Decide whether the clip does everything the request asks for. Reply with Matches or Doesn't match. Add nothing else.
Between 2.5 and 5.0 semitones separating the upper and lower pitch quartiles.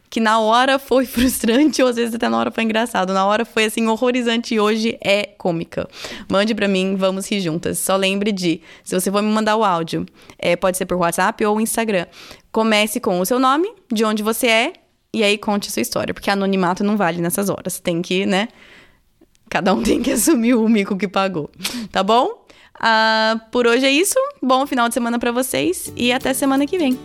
Matches